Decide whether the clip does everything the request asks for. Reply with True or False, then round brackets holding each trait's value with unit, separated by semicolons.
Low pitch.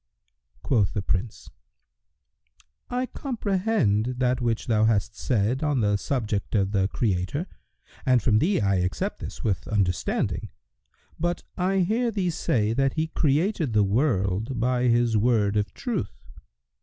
True (120 Hz)